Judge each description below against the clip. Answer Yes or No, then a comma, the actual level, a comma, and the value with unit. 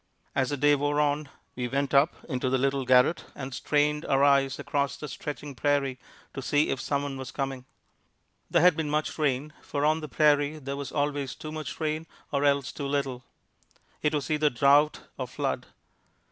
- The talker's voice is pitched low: No, medium, 145 Hz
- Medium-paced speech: Yes, average, 190 wpm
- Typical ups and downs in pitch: No, narrow, 1.6 semitones